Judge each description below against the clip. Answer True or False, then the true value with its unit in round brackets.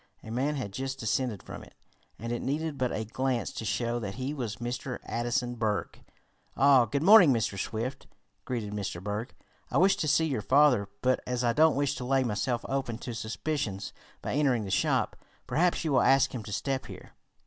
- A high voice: False (125 Hz)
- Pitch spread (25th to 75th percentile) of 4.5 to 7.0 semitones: False (3.5 semitones)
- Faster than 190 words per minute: True (200 wpm)